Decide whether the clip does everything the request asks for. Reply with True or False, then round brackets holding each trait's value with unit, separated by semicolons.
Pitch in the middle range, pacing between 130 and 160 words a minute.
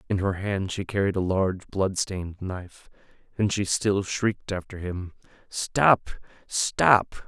False (95 Hz; 150 wpm)